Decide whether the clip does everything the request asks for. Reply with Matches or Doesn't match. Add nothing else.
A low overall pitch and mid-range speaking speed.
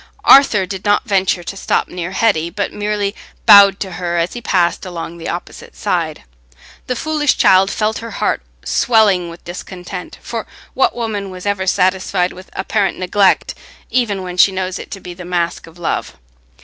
Doesn't match